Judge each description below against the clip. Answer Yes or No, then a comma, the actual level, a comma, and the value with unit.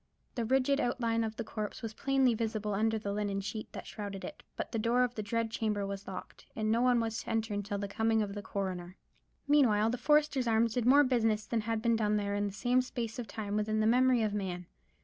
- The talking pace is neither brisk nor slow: No, fast, 240 wpm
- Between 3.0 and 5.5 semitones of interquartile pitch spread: No, narrow, 2.6 semitones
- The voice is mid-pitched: No, high, 220 Hz